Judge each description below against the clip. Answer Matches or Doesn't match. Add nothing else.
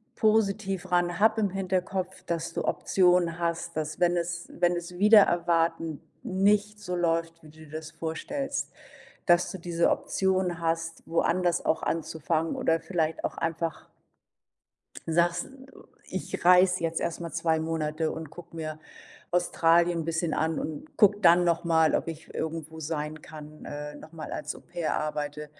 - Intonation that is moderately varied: Doesn't match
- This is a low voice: Doesn't match